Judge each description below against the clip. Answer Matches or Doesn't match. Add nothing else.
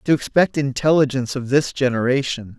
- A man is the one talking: Matches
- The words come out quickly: Doesn't match